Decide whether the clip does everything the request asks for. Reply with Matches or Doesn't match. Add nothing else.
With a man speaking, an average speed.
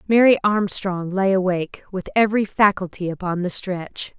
Doesn't match